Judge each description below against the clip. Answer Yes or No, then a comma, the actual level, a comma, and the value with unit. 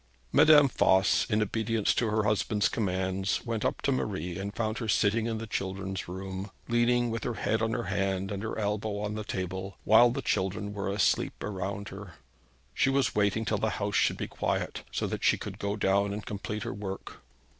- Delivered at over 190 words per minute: Yes, average, 200 wpm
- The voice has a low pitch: Yes, low, 105 Hz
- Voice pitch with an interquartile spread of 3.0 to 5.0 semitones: No, narrow, 2.4 semitones